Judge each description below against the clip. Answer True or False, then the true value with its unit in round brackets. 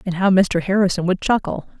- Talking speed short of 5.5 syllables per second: False (5.6 syllables/s)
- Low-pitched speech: False (185 Hz)